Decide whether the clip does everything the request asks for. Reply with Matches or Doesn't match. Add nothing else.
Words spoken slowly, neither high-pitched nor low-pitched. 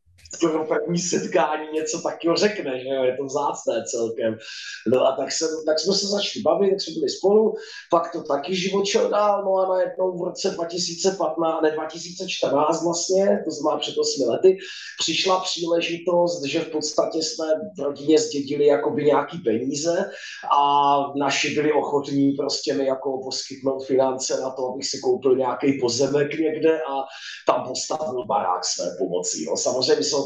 Doesn't match